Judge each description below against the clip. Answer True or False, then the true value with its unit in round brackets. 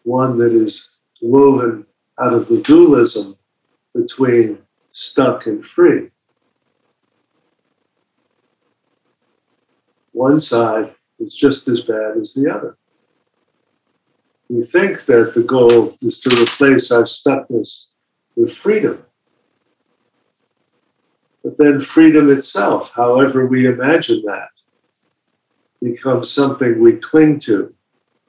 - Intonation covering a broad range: True (7.8 semitones)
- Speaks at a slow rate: True (100 wpm)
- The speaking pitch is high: False (140 Hz)